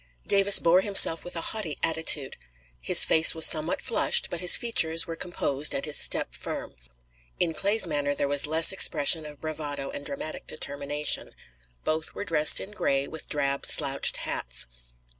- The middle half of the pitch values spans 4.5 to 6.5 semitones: No, average, 3.6 semitones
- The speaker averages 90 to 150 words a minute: No, average, 165 wpm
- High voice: No, medium, 160 Hz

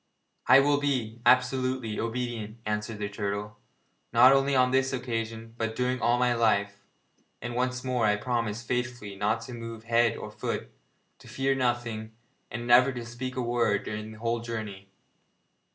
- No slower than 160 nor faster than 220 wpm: Yes, average, 165 wpm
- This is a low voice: Yes, low, 120 Hz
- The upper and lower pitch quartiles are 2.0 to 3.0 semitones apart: Yes, narrow, 2.5 semitones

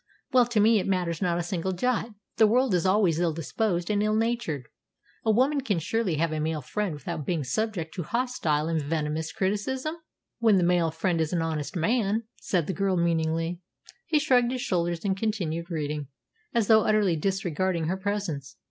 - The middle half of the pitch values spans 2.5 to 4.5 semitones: No, average, 4.9 semitones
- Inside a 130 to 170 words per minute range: No, average, 190 wpm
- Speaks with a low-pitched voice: No, medium, 185 Hz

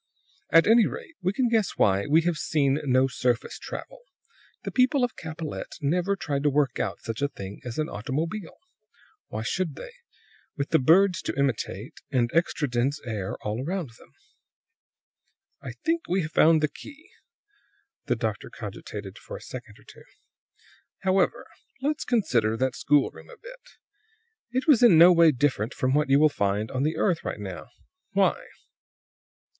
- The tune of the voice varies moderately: No, wide, 7.0 semitones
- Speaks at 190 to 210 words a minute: No, average, 165 wpm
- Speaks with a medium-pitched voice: Yes, medium, 150 Hz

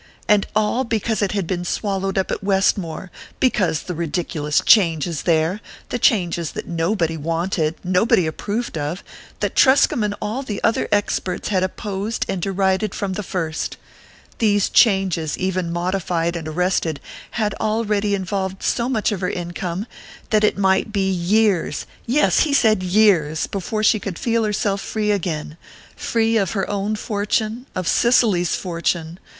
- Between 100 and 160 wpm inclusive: Yes, average, 155 wpm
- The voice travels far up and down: No, average, 3.5 semitones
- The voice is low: No, high, 195 Hz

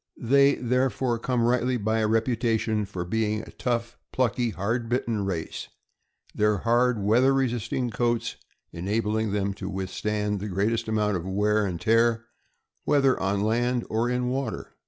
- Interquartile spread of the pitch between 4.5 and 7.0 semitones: No, average, 2.8 semitones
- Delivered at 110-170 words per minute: Yes, average, 155 wpm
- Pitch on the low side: Yes, low, 115 Hz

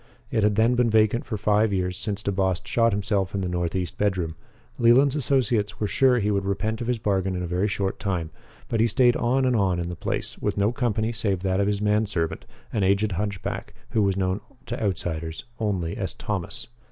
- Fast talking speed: Yes, fast, 220 wpm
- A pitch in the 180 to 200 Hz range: No, low, 100 Hz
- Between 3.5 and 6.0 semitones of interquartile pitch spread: No, average, 3.0 semitones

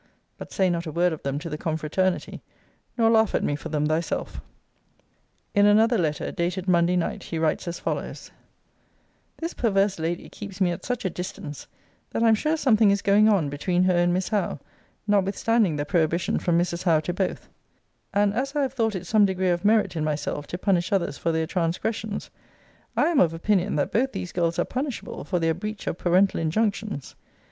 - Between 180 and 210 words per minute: Yes, average, 200 wpm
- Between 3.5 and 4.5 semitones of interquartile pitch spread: Yes, average, 4.0 semitones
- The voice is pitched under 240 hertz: Yes, medium, 185 Hz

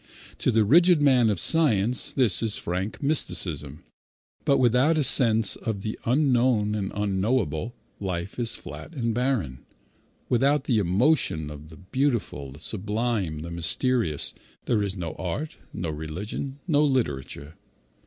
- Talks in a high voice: No, low, 110 Hz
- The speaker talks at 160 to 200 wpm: No, average, 140 wpm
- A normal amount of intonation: No, wide, 7.0 semitones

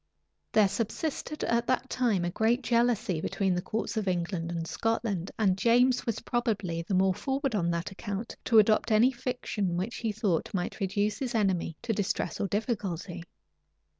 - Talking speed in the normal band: Yes, average, 175 wpm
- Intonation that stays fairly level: No, average, 4.3 semitones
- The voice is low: No, high, 210 Hz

